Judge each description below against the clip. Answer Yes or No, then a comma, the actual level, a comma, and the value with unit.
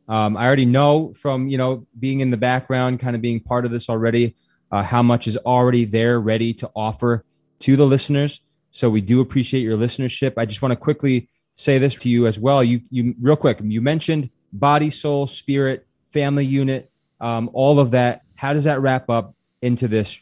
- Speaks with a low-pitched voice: Yes, low, 125 Hz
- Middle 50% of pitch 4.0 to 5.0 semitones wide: No, average, 2.8 semitones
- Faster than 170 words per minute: Yes, fast, 205 wpm